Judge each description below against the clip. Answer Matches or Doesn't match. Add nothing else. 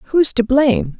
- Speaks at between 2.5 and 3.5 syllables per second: Doesn't match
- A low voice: Doesn't match